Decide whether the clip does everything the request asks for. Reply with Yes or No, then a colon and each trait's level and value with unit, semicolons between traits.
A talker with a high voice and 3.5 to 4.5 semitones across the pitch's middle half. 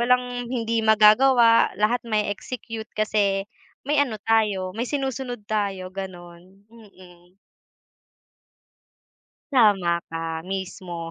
Yes: high, 210 Hz; average, 4.1 semitones